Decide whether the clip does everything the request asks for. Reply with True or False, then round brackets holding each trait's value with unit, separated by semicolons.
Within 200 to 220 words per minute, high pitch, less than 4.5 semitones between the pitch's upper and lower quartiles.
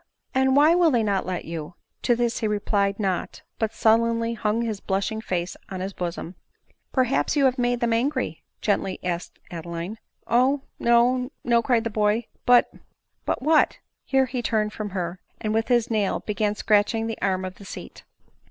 True (205 wpm; 220 Hz; 3.8 semitones)